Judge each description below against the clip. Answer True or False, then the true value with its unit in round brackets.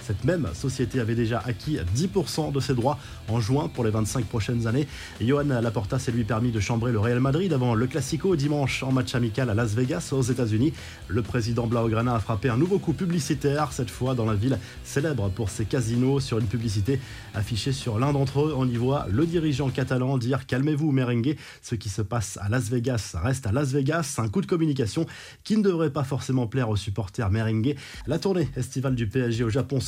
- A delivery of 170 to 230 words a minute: True (215 wpm)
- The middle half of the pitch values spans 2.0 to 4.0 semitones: True (3.5 semitones)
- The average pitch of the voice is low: True (130 Hz)